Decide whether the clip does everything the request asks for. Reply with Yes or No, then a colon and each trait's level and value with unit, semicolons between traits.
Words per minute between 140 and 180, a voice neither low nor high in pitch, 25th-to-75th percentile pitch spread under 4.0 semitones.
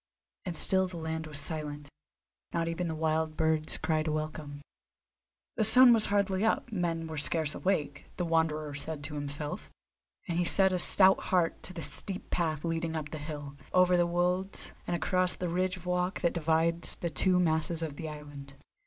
No: average, 190 wpm; medium, 165 Hz; average, 2.7 semitones